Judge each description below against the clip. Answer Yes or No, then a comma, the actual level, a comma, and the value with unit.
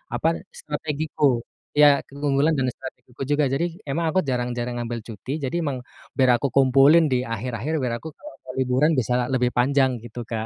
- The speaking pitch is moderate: No, low, 130 Hz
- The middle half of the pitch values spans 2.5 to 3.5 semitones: Yes, average, 2.8 semitones